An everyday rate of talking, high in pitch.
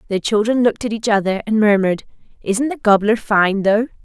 Yes: average, 195 wpm; high, 215 Hz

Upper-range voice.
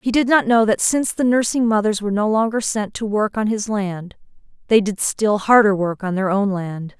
Yes: high, 210 Hz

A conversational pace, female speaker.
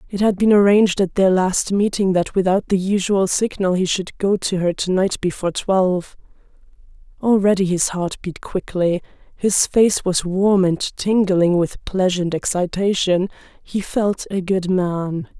Yes: average, 160 wpm; female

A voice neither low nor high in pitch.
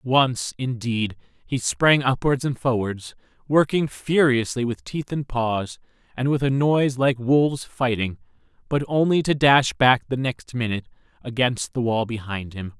No: low, 125 Hz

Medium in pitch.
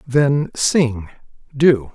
No: low, 130 Hz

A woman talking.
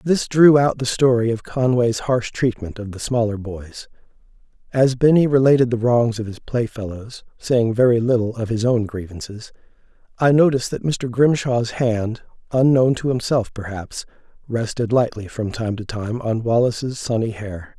No: male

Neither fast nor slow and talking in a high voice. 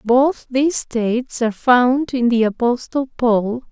Yes: average, 145 wpm; high, 245 Hz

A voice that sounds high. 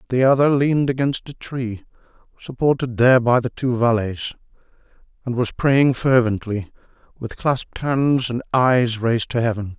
No: low, 125 Hz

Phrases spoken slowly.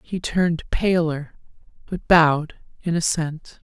Yes: slow, 115 wpm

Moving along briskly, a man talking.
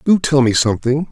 Yes: fast, 215 wpm; male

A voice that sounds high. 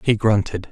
No: low, 105 Hz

